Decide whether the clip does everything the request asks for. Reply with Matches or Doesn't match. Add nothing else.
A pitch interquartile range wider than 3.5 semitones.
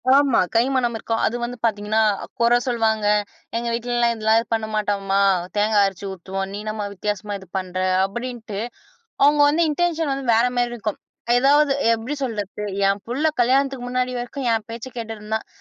Doesn't match